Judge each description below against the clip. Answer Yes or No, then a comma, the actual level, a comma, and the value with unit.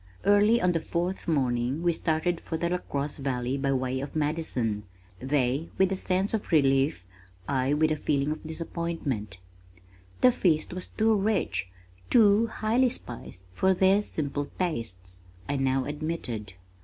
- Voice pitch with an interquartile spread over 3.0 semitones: Yes, wide, 5.6 semitones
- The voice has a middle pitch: Yes, medium, 155 Hz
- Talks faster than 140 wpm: Yes, average, 150 wpm